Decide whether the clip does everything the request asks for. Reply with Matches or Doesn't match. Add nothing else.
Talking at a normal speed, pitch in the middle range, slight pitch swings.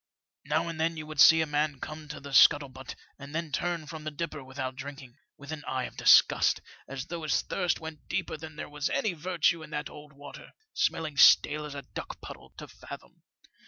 Doesn't match